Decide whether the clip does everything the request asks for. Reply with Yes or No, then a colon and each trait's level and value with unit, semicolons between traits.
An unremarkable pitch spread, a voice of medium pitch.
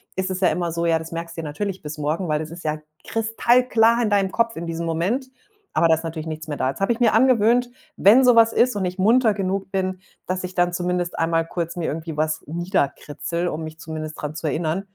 Yes: average, 4.2 semitones; medium, 175 Hz